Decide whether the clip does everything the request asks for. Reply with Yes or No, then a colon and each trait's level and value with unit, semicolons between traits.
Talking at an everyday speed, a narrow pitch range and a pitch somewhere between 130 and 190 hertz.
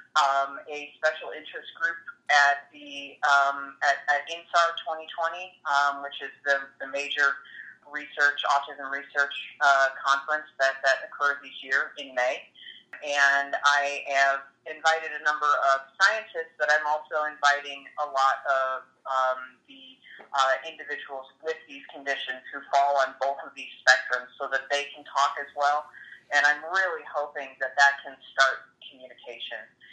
Yes: average, 150 wpm; narrow, 1.8 semitones; medium, 140 Hz